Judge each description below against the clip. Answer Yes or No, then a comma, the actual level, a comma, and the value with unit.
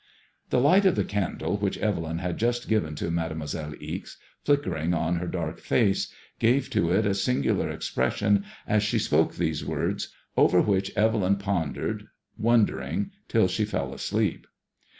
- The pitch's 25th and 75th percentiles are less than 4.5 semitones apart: No, average, 4.8 semitones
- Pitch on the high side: No, low, 100 Hz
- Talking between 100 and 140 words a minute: No, average, 160 wpm